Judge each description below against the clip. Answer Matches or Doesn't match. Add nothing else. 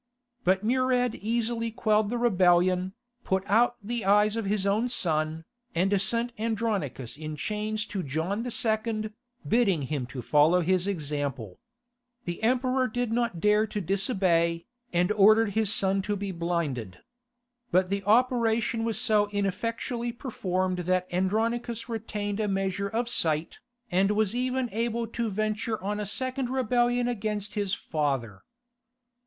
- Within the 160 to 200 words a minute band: Doesn't match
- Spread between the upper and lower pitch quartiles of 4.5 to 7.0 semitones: Doesn't match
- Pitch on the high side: Matches